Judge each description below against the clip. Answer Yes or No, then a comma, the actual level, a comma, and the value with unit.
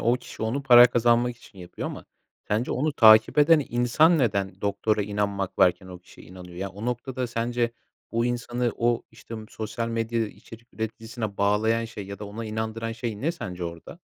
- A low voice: Yes, low, 115 Hz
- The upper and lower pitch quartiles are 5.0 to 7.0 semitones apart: No, average, 2.8 semitones